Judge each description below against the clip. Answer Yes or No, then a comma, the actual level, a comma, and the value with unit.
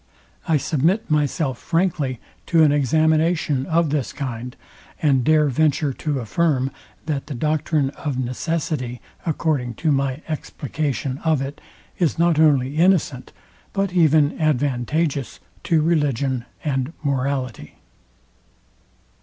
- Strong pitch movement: No, average, 3.1 semitones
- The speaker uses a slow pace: Yes, slow, 115 wpm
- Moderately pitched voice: Yes, medium, 145 Hz